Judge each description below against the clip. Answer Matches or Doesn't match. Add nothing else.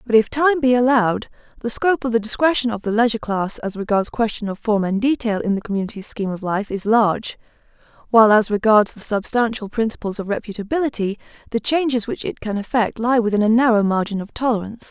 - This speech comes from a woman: Matches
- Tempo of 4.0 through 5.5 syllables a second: Doesn't match